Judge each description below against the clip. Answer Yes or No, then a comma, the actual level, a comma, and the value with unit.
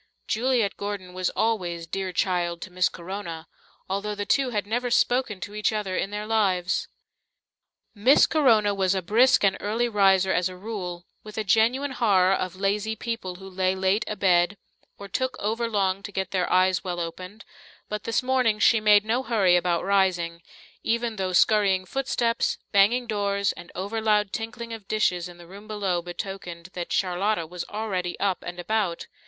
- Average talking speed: Yes, average, 175 wpm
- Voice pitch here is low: No, high, 200 Hz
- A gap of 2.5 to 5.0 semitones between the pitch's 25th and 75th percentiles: Yes, average, 3.1 semitones